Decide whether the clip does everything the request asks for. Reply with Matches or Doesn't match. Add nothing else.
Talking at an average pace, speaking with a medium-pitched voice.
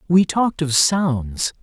Matches